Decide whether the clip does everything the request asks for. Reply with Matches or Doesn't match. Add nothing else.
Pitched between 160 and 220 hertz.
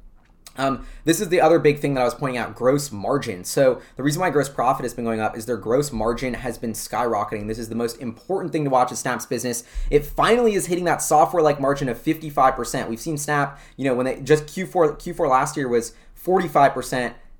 Doesn't match